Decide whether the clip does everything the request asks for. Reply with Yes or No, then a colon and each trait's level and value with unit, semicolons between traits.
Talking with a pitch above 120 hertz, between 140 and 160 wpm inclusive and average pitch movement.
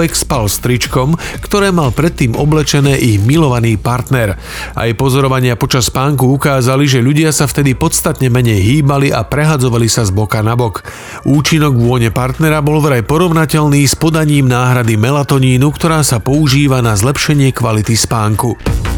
Yes: low, 135 Hz; average, 145 wpm; average, 3.9 semitones